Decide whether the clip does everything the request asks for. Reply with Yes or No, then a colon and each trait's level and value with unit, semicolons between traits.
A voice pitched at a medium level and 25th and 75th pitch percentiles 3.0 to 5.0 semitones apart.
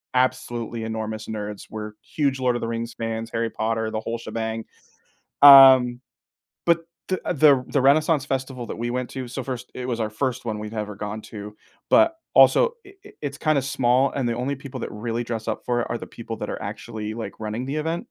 No: low, 120 Hz; average, 3.3 semitones